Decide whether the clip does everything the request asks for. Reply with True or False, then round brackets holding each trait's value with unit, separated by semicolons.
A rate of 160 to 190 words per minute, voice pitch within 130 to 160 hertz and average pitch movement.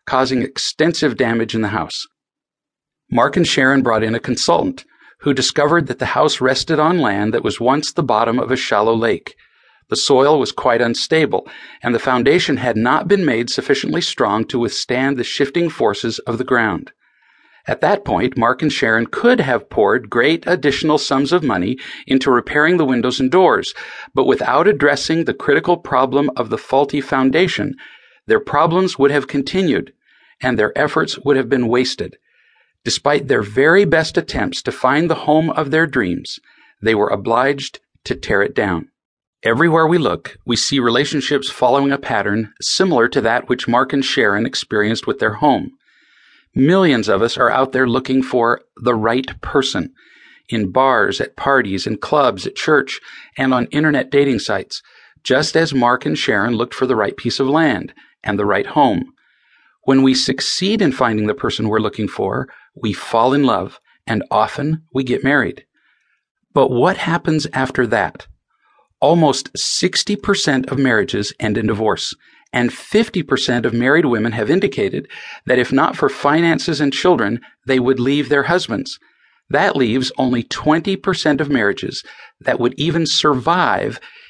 True (165 wpm; 135 Hz; 4.0 semitones)